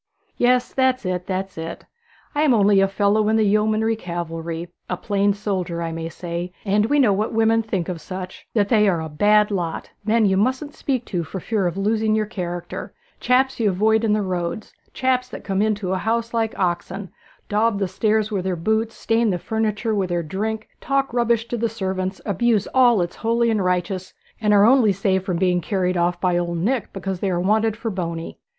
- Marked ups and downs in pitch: No, average, 3.5 semitones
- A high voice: Yes, high, 205 Hz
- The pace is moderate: No, fast, 210 wpm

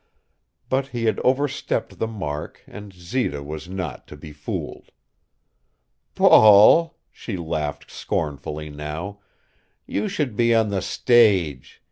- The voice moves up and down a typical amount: No, wide, 7.2 semitones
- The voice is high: No, low, 100 Hz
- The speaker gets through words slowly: Yes, slow, 120 wpm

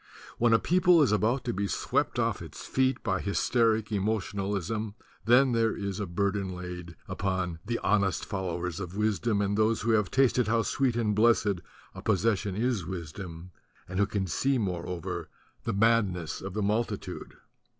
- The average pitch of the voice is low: Yes, low, 105 Hz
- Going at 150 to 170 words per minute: Yes, average, 165 wpm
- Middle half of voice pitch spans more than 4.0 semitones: No, average, 3.6 semitones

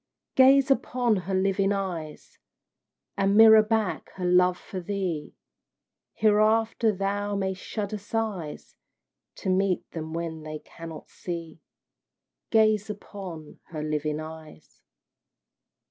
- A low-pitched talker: No, high, 195 Hz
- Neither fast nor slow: No, slow, 110 wpm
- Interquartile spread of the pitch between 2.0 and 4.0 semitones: No, average, 4.4 semitones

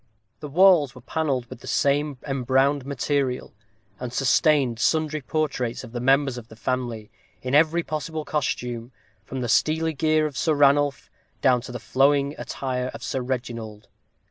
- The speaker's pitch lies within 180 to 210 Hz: No, low, 135 Hz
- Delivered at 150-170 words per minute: Yes, average, 160 wpm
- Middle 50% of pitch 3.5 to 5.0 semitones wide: No, average, 3.1 semitones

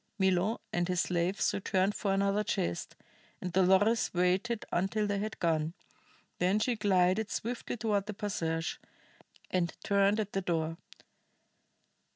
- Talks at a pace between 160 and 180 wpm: No, slow, 135 wpm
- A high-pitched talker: Yes, high, 195 Hz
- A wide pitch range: No, average, 2.7 semitones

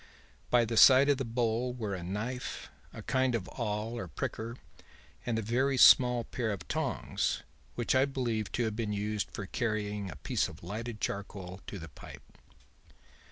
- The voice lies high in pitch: No, low, 115 Hz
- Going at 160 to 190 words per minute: Yes, average, 175 wpm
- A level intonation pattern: No, average, 3.0 semitones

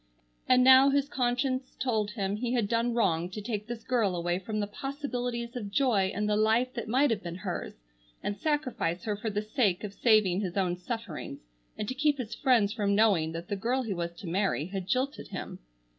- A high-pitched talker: Yes, high, 215 Hz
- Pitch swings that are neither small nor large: Yes, average, 4.3 semitones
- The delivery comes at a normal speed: No, fast, 210 wpm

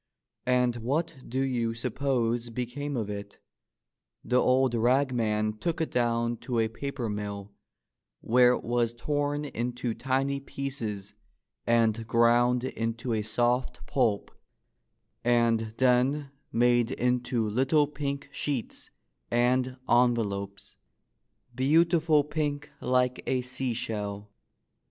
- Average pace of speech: No, slow, 115 wpm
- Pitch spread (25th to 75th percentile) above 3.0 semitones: No, average, 2.7 semitones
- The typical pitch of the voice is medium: No, low, 125 Hz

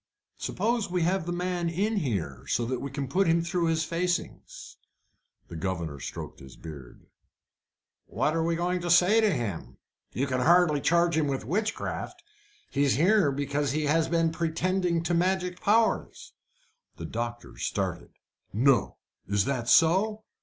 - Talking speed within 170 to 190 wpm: No, average, 160 wpm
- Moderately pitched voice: Yes, medium, 165 Hz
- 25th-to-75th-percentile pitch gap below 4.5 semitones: No, average, 5.1 semitones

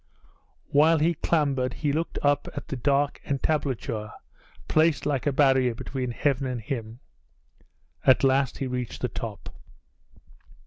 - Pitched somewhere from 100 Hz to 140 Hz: Yes, low, 135 Hz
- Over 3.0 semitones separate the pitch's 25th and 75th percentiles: No, narrow, 2.5 semitones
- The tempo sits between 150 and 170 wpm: No, slow, 135 wpm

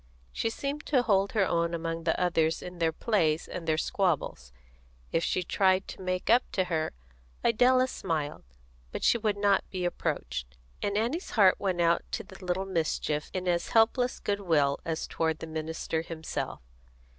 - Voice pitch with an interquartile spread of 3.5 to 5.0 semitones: Yes, average, 3.8 semitones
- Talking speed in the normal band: Yes, average, 170 wpm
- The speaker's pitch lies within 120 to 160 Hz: No, medium, 180 Hz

